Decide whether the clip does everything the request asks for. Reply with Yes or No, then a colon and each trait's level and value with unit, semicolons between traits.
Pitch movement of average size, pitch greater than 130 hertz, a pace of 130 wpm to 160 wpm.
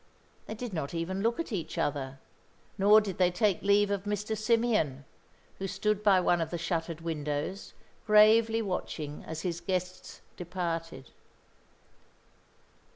Yes: average, 4.1 semitones; medium, 185 Hz; average, 140 wpm